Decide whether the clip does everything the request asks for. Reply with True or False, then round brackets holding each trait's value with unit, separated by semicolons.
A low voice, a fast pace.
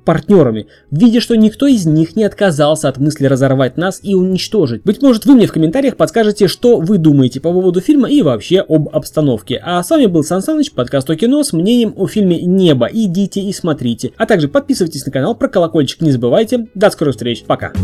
False (180 Hz; 210 wpm)